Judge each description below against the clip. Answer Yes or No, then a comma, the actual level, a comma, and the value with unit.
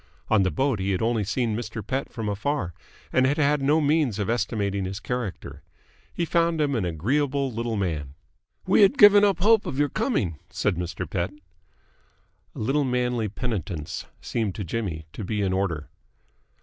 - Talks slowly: No, average, 180 wpm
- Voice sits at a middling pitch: No, low, 115 Hz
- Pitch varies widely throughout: Yes, wide, 6.6 semitones